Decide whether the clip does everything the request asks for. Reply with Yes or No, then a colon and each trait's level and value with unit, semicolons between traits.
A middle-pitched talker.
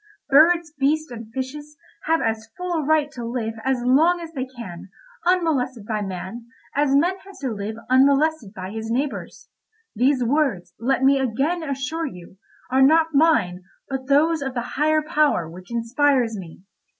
No: very high, 270 Hz